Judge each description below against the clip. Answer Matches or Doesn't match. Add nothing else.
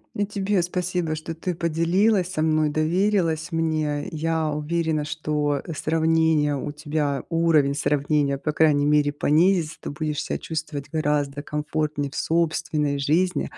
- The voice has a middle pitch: Matches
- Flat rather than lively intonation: Matches